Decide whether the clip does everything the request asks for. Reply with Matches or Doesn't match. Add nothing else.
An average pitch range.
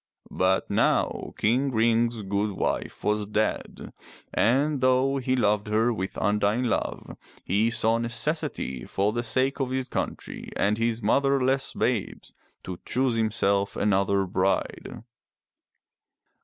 Matches